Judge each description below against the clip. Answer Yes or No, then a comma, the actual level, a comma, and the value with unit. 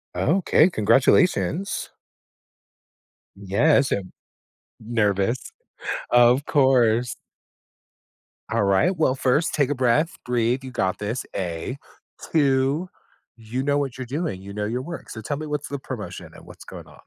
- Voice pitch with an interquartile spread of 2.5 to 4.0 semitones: No, average, 4.7 semitones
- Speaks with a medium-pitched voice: No, low, 130 Hz